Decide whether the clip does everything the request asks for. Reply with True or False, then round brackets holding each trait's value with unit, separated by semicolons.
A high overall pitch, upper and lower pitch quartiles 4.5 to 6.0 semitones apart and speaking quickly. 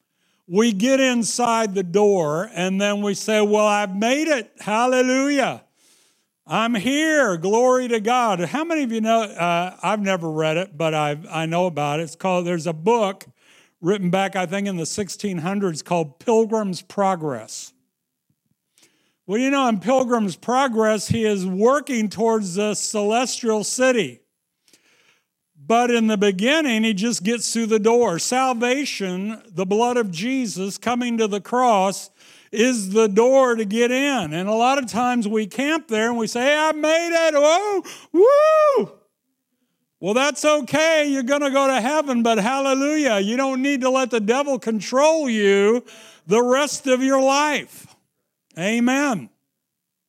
False (225 Hz; 4.8 semitones; 155 wpm)